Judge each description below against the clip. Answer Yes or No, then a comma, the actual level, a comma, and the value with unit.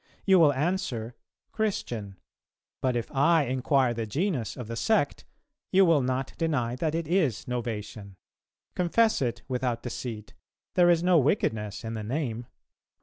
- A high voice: No, low, 130 Hz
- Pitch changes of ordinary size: No, wide, 6.1 semitones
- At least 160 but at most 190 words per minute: No, average, 145 wpm